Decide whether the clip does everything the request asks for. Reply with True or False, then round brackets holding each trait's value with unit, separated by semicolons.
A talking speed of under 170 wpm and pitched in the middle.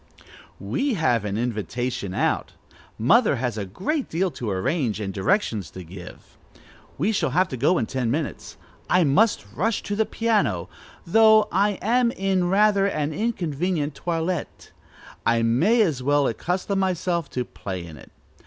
True (155 wpm; 160 Hz)